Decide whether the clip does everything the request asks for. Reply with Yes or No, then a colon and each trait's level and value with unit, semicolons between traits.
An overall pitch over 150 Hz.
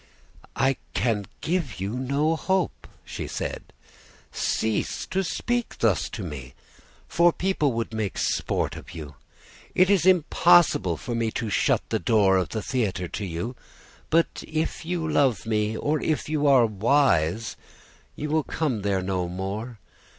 No: low, 115 Hz